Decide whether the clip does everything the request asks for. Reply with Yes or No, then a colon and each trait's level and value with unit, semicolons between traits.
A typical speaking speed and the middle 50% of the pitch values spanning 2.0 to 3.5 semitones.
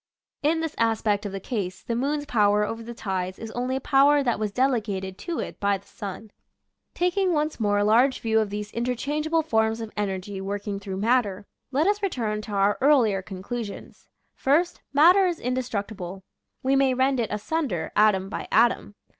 No: average, 180 wpm; average, 5.1 semitones